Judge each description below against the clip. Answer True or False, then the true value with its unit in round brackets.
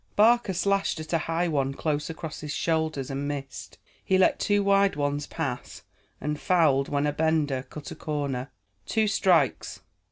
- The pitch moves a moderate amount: True (4.1 semitones)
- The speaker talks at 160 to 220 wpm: True (165 wpm)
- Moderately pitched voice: True (155 Hz)